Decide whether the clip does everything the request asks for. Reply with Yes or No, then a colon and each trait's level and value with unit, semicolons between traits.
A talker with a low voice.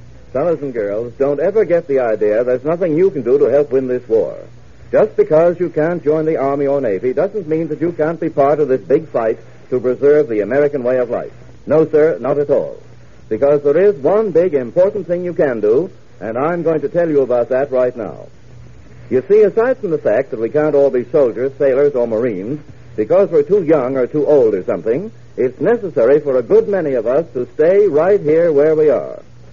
No: medium, 170 Hz